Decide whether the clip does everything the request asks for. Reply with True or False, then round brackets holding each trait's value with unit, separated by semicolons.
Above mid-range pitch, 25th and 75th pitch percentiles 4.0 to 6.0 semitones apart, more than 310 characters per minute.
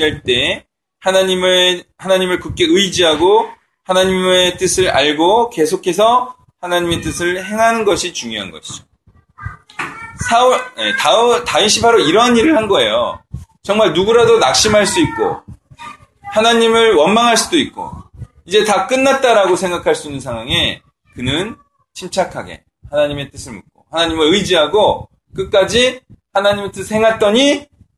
False (195 Hz; 5.1 semitones; 295 characters per minute)